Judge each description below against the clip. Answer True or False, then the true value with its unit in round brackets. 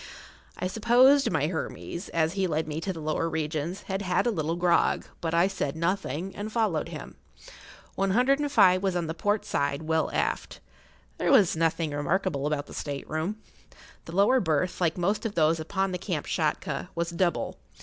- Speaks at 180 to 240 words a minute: True (185 wpm)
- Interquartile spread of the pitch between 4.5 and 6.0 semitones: False (3.5 semitones)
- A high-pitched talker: False (170 Hz)